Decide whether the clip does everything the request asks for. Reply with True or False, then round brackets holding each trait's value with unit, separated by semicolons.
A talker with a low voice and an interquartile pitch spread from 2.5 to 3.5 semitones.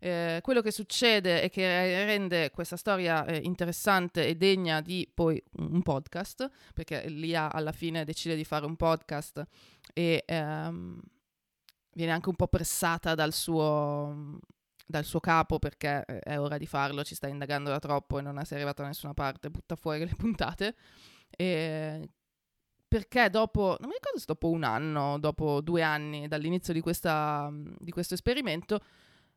False (160 Hz; 2.9 semitones)